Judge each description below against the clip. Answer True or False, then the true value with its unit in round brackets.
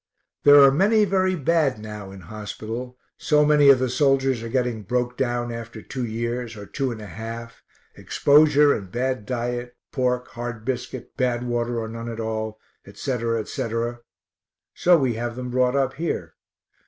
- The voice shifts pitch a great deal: False (2.7 semitones)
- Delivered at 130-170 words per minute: True (165 wpm)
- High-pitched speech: False (120 Hz)